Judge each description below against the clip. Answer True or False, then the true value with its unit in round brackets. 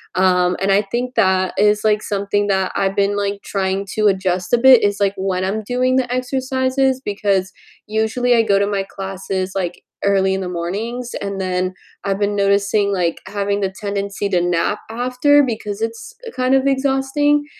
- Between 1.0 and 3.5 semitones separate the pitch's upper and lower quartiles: False (4.2 semitones)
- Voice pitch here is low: False (200 Hz)